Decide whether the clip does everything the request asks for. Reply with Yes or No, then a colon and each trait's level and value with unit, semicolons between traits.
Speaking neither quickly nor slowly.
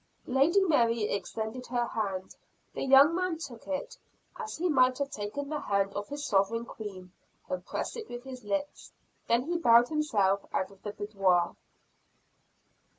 Yes: average, 160 wpm